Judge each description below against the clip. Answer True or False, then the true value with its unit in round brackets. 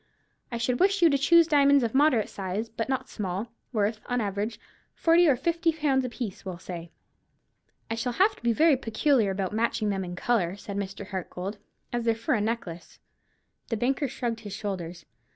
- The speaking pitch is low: False (230 Hz)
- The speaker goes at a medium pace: True (190 wpm)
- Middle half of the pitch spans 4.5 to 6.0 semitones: True (5.1 semitones)